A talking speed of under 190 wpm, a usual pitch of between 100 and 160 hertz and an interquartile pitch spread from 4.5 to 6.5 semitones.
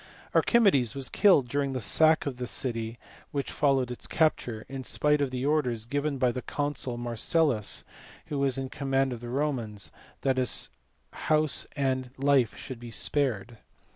No: average, 165 wpm; low, 135 Hz; average, 2.9 semitones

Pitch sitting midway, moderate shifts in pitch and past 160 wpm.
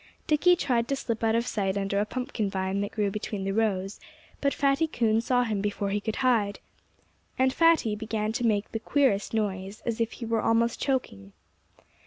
No: high, 220 Hz; average, 3.5 semitones; average, 195 wpm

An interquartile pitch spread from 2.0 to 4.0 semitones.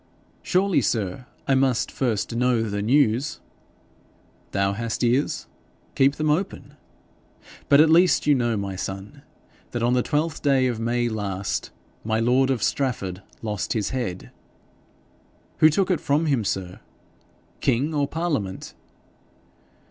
No: average, 5.2 semitones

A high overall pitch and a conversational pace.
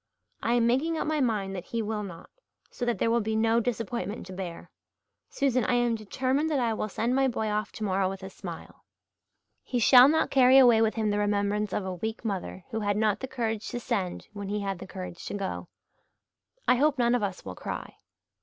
No: high, 220 Hz; fast, 220 wpm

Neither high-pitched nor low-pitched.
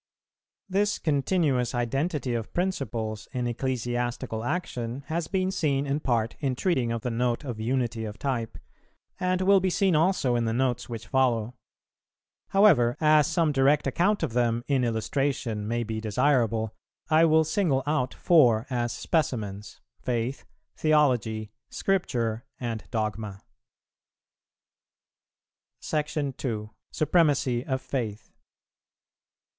No: low, 125 Hz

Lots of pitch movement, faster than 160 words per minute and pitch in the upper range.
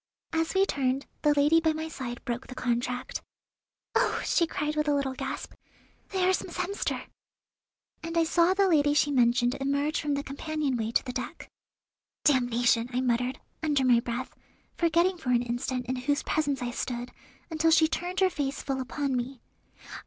No: average, 4.1 semitones; average, 180 wpm; very high, 280 Hz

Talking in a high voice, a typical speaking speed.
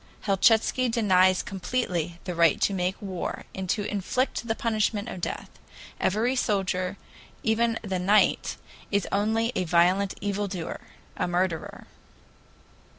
No: high, 200 Hz; slow, 130 wpm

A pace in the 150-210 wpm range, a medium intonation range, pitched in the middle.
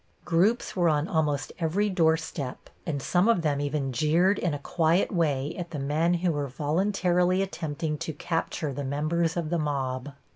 Yes: average, 175 wpm; average, 3.3 semitones; medium, 160 Hz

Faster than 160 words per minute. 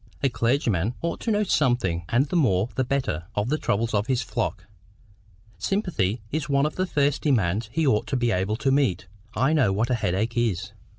Yes: average, 195 wpm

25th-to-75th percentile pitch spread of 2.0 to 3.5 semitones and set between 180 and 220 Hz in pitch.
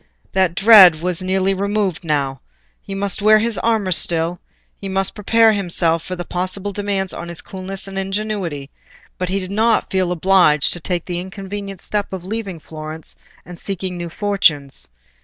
Yes: narrow, 2.6 semitones; high, 190 Hz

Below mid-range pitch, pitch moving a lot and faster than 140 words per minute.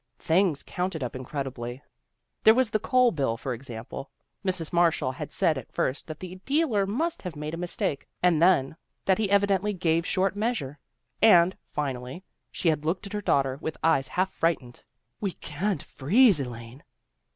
No: medium, 165 Hz; wide, 6.1 semitones; average, 175 wpm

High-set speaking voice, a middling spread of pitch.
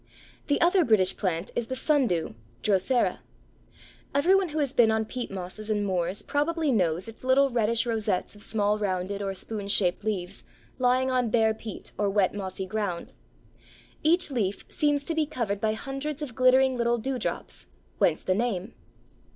Yes: high, 220 Hz; average, 4.9 semitones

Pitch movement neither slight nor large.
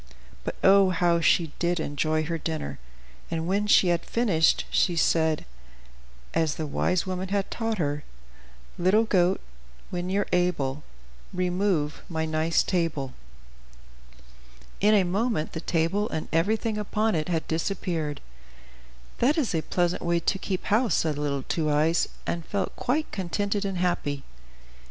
Yes: average, 3.7 semitones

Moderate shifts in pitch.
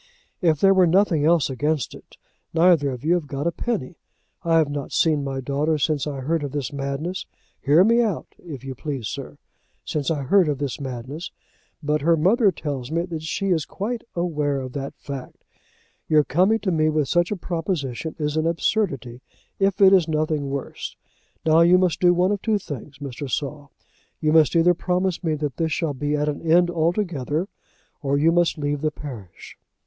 Yes: average, 3.5 semitones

